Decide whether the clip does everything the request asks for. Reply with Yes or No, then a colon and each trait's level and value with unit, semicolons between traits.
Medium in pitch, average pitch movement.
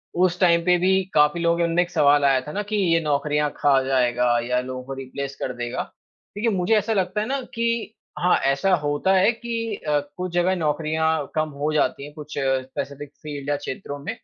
Yes: medium, 155 Hz; average, 4.7 semitones